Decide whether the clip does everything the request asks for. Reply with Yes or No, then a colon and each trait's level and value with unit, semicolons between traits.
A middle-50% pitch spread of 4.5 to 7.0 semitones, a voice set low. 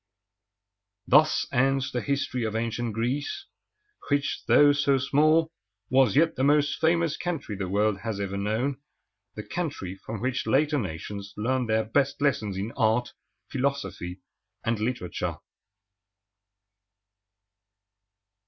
Yes: average, 4.9 semitones; low, 125 Hz